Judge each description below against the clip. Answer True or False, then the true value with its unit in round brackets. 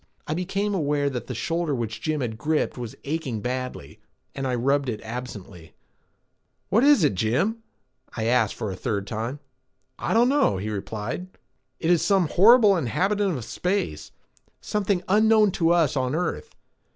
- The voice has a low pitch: False (145 Hz)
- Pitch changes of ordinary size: False (8.6 semitones)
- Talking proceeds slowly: False (165 wpm)